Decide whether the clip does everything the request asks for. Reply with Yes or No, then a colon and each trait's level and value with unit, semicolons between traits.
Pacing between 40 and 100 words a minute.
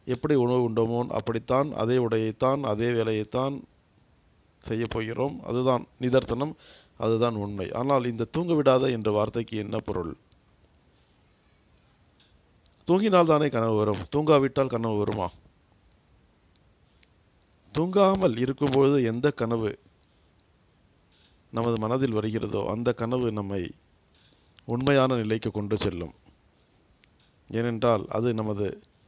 Yes: average, 95 wpm